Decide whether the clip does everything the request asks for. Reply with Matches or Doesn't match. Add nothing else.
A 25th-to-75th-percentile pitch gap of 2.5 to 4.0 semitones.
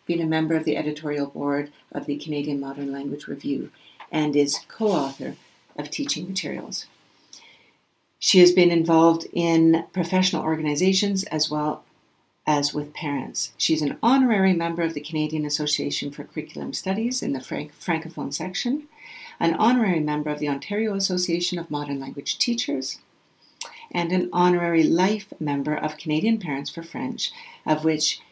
Matches